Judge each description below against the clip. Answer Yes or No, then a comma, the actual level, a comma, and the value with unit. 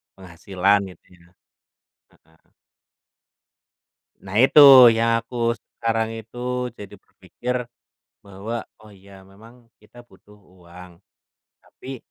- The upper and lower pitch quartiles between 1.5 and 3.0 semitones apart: No, average, 3.7 semitones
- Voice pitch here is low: Yes, low, 100 Hz